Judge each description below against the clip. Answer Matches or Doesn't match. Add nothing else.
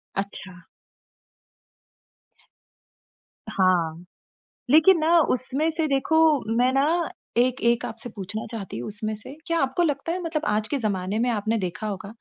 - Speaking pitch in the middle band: Doesn't match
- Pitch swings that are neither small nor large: Doesn't match